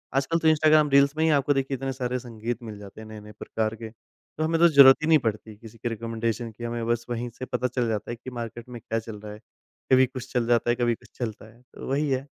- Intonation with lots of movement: No, average, 3.0 semitones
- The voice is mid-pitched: No, low, 120 Hz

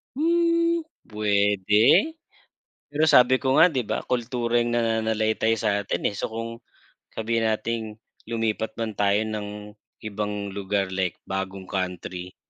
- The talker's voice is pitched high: No, low, 110 Hz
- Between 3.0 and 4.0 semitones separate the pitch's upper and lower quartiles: No, narrow, 2.5 semitones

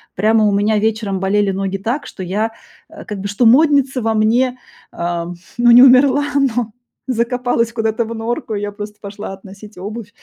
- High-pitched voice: Yes, high, 220 Hz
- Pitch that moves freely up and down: No, average, 3.0 semitones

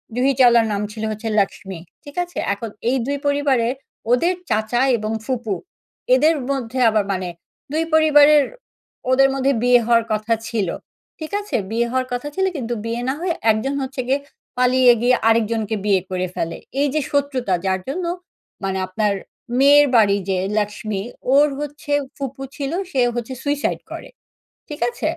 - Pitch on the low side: No, high, 245 Hz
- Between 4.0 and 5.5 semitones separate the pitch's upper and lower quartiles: Yes, average, 4.7 semitones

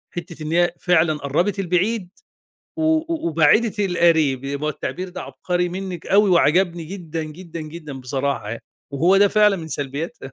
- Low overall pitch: No, medium, 170 Hz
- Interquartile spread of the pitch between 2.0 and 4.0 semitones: Yes, average, 3.6 semitones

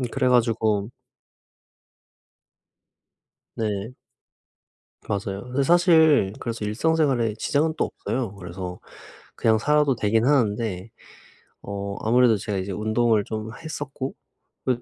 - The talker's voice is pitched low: Yes, low, 115 Hz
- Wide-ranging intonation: No, average, 4.3 semitones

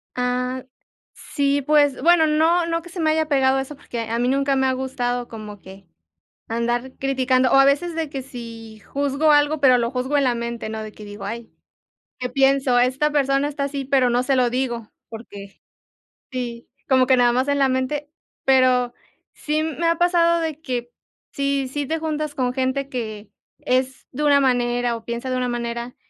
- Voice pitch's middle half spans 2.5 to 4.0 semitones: Yes, average, 2.9 semitones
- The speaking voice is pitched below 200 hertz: No, very high, 260 Hz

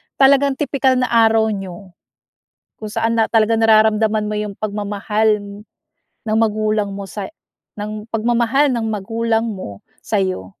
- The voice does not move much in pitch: Yes, narrow, 1.7 semitones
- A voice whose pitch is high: Yes, high, 215 Hz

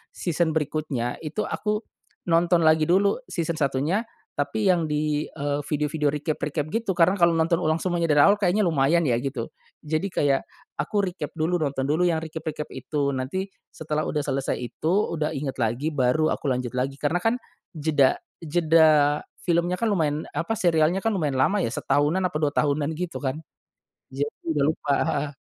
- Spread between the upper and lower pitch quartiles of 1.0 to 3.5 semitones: Yes, average, 3.2 semitones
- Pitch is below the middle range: No, medium, 155 Hz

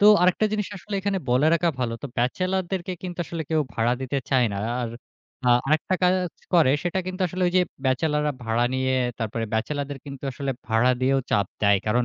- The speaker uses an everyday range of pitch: No, wide, 6.6 semitones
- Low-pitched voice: No, medium, 145 Hz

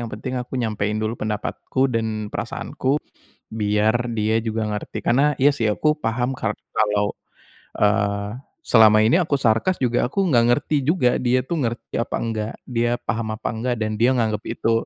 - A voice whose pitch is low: Yes, low, 115 Hz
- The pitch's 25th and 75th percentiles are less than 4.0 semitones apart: Yes, average, 2.8 semitones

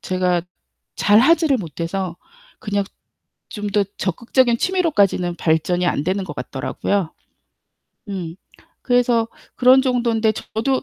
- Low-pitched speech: No, high, 205 Hz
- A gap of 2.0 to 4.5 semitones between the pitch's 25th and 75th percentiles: No, wide, 5.5 semitones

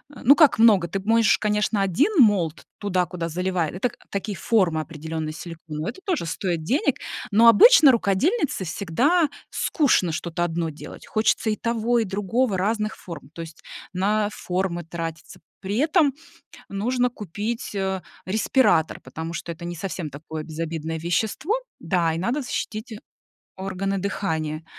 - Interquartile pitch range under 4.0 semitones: No, average, 5.1 semitones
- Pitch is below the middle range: No, high, 190 Hz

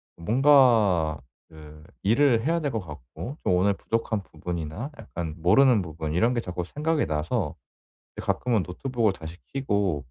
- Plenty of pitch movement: Yes, wide, 7.4 semitones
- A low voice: Yes, low, 100 Hz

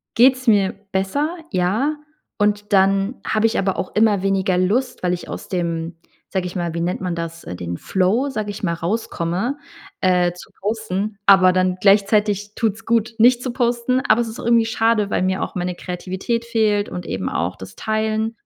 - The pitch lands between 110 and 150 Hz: No, high, 200 Hz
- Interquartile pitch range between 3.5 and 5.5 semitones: Yes, average, 3.8 semitones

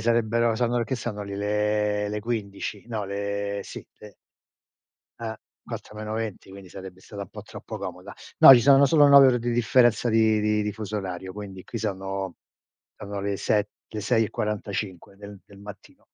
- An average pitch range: No, narrow, 2.2 semitones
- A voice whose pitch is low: Yes, low, 105 Hz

